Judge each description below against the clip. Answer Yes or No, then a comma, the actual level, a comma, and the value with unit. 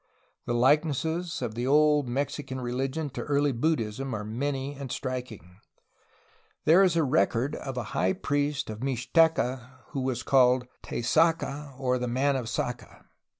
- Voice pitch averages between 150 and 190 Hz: No, low, 130 Hz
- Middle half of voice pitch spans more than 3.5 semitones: No, average, 3.0 semitones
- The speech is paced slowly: No, average, 150 wpm